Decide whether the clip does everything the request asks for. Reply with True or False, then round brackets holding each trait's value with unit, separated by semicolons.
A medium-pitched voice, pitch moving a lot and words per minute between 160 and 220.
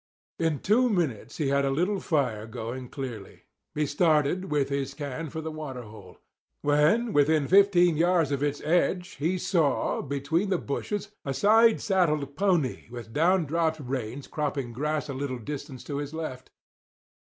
False (150 Hz; 4.2 semitones; 165 wpm)